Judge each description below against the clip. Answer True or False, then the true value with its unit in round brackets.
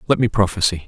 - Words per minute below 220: True (205 wpm)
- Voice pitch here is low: True (100 Hz)